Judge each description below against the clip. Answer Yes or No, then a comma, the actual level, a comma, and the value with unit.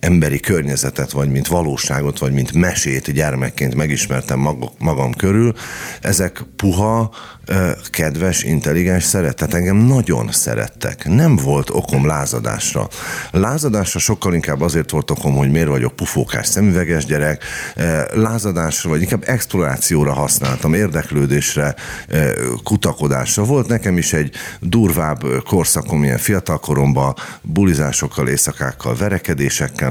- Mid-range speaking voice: No, very low, 80 Hz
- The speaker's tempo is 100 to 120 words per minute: Yes, average, 110 wpm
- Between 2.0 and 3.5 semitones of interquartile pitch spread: No, wide, 5.6 semitones